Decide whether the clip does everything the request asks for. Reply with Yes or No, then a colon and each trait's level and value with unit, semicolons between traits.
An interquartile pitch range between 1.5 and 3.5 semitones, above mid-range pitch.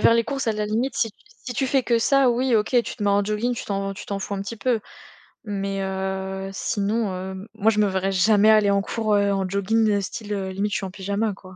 Yes: narrow, 2.5 semitones; high, 205 Hz